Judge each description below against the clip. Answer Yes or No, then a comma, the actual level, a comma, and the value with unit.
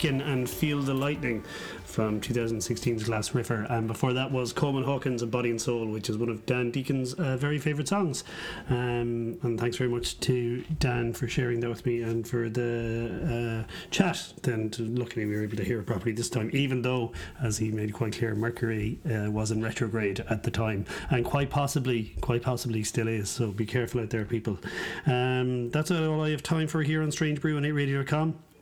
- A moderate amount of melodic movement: Yes, average, 3.2 semitones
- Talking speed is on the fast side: Yes, fast, 210 wpm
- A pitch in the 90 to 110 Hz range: No, low, 120 Hz